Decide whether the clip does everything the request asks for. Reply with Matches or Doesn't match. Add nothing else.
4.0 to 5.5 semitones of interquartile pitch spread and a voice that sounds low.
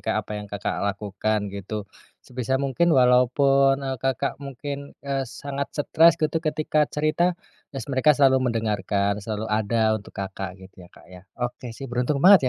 Matches